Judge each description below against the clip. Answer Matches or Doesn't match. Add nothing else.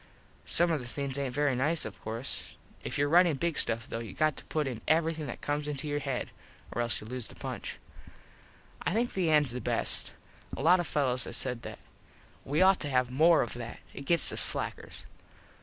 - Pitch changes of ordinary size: Matches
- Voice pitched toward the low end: Doesn't match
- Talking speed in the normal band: Doesn't match